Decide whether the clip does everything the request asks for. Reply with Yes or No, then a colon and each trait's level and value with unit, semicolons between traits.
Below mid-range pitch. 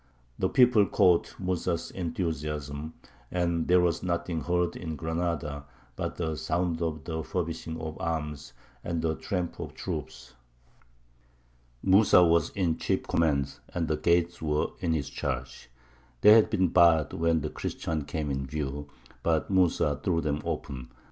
Yes: very low, 80 Hz